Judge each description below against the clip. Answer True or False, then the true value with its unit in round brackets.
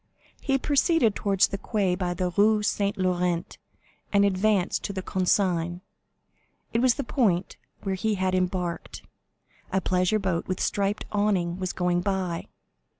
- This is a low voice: False (190 Hz)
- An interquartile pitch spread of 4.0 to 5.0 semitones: False (2.5 semitones)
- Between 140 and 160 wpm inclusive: True (150 wpm)